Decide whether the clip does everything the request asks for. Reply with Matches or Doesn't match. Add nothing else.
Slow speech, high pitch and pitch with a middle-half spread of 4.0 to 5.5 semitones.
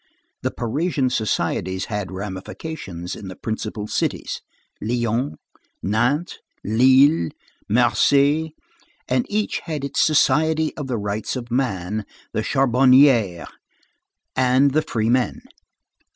Doesn't match